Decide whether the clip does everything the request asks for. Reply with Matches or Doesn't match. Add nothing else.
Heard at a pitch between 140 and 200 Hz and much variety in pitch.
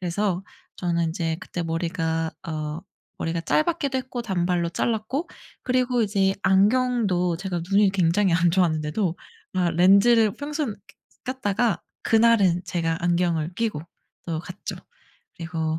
Doesn't match